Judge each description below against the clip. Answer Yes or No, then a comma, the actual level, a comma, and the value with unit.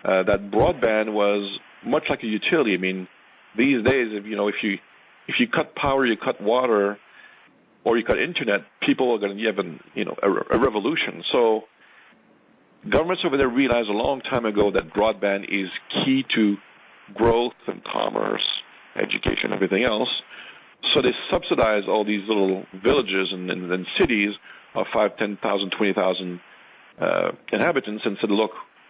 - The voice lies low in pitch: Yes, low, 105 Hz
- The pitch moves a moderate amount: No, narrow, 2.3 semitones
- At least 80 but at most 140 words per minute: No, average, 165 wpm